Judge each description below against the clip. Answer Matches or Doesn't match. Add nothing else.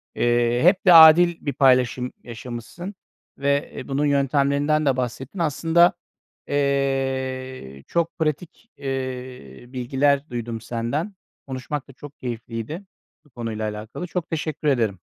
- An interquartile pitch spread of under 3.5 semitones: Doesn't match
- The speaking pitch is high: Doesn't match